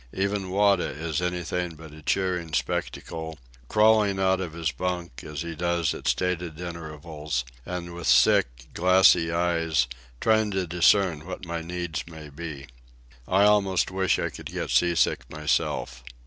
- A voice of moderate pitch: No, very low, 85 Hz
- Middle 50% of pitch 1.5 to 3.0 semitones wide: Yes, average, 2.7 semitones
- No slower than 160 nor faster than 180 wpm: No, average, 150 wpm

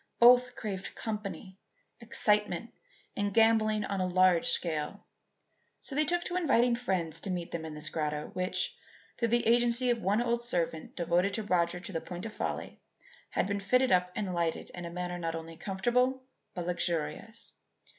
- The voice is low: No, high, 195 Hz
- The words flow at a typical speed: Yes, average, 175 wpm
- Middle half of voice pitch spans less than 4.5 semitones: No, average, 5.2 semitones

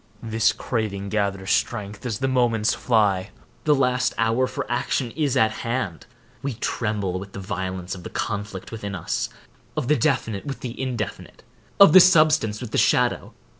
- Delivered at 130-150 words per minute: No, average, 160 wpm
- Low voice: Yes, low, 110 Hz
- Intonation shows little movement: No, average, 4.2 semitones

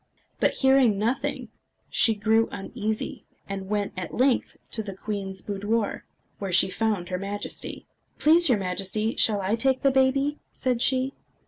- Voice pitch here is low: No, high, 215 Hz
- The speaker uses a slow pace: No, average, 150 wpm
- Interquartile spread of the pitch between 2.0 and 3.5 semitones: No, average, 4.6 semitones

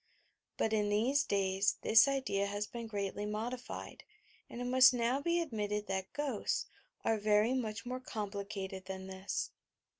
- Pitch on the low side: No, high, 215 Hz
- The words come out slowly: No, average, 155 wpm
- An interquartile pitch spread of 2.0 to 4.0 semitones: Yes, average, 3.7 semitones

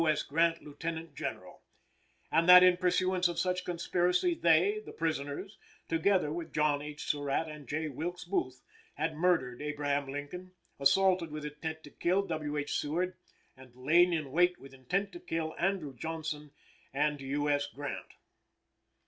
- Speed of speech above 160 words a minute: No, average, 155 wpm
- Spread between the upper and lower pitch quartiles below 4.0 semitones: Yes, average, 3.5 semitones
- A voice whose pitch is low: No, medium, 160 Hz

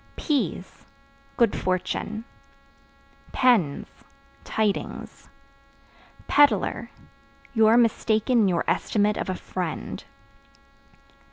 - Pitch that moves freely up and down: No, average, 4.1 semitones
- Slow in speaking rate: Yes, slow, 80 wpm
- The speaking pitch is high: Yes, high, 215 Hz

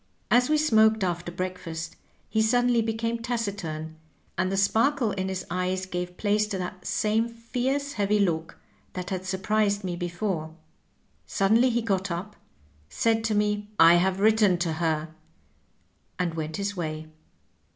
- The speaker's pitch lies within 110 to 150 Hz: No, high, 195 Hz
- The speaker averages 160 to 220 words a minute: No, average, 150 wpm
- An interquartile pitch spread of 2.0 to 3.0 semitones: No, average, 3.8 semitones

